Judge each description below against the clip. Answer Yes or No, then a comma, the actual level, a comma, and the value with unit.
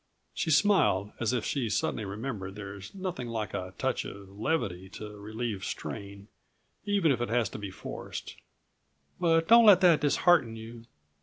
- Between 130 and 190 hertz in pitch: No, low, 115 Hz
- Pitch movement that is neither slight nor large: No, wide, 8.1 semitones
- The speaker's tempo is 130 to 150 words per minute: No, average, 160 wpm